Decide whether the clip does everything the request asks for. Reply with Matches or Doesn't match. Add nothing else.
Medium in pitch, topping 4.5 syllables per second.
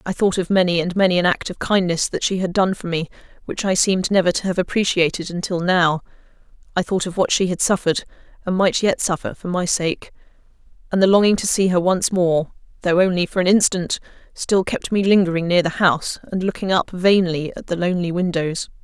Matches